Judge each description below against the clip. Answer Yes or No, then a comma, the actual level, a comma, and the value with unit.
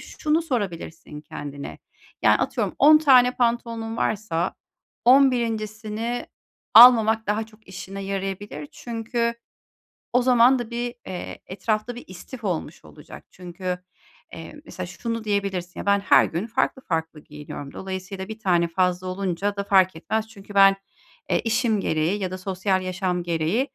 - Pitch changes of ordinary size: Yes, average, 4.2 semitones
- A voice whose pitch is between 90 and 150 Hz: No, high, 200 Hz